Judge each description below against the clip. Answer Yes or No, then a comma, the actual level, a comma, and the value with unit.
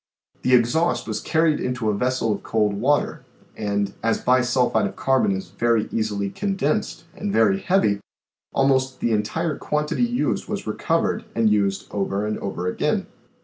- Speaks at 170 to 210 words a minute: No, average, 160 wpm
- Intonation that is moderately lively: No, wide, 5.9 semitones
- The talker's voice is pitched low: Yes, low, 115 Hz